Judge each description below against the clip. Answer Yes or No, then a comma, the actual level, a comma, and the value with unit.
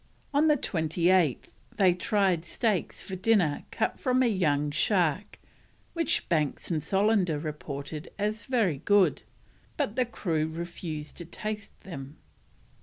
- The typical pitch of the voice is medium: Yes, medium, 180 Hz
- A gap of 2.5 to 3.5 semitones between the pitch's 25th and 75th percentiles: No, average, 5.3 semitones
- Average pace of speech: No, slow, 130 wpm